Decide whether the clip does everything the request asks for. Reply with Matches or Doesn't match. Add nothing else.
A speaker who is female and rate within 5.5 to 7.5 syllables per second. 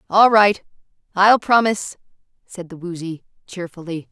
Doesn't match